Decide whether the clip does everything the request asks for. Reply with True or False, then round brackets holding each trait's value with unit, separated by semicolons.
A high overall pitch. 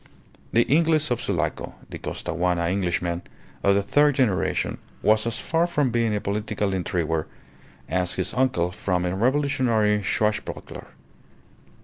False (105 Hz)